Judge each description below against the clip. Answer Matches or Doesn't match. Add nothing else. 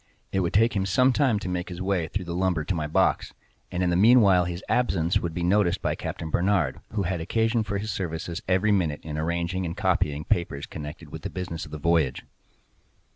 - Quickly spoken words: Matches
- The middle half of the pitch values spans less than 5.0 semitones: Matches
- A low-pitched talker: Matches